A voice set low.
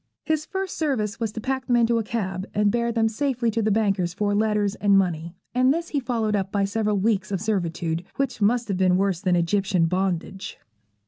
No: high, 210 Hz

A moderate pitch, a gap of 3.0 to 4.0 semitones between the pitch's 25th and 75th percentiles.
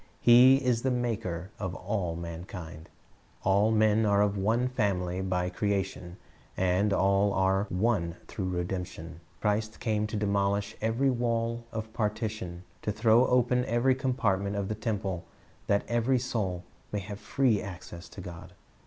No: low, 105 Hz; average, 3.6 semitones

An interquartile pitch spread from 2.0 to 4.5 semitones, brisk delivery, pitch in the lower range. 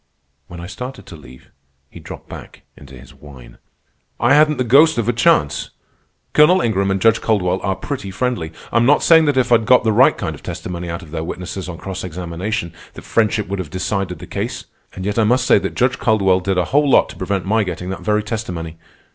No: average, 5.1 semitones; fast, 225 wpm; low, 100 Hz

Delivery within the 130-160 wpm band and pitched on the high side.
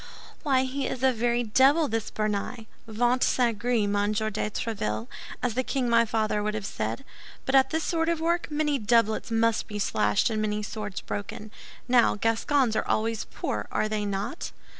No: average, 185 wpm; high, 225 Hz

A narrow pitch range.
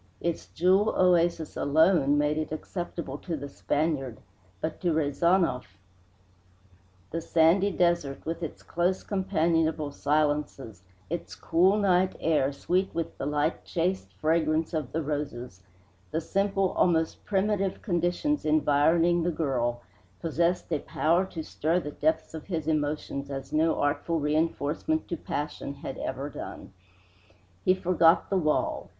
No: average, 3.1 semitones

